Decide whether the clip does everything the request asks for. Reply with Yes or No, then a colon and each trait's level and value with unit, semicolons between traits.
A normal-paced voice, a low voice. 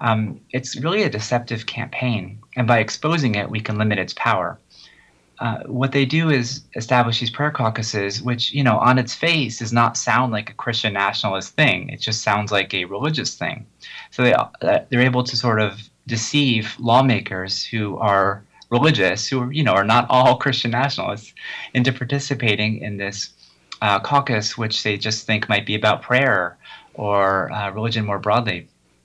Yes: average, 180 wpm; low, 115 Hz